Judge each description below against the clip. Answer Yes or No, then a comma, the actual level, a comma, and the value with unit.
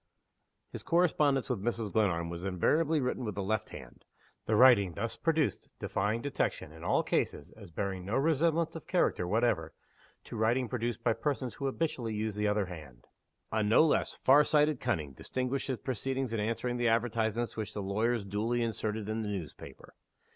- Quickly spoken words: No, average, 175 wpm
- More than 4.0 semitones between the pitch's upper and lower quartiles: Yes, average, 4.5 semitones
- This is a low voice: Yes, low, 115 Hz